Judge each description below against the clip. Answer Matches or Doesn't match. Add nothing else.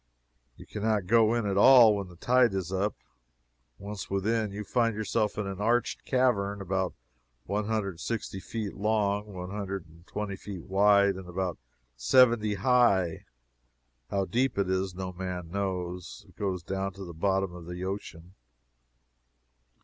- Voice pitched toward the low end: Matches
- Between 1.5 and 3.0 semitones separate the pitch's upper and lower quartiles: Matches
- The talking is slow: Doesn't match